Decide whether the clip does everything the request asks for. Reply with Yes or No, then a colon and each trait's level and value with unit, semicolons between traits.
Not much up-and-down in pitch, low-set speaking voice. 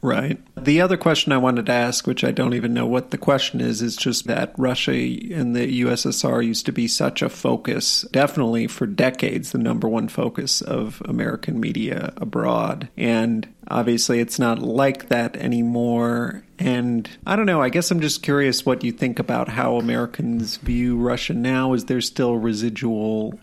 Yes: narrow, 1.7 semitones; low, 120 Hz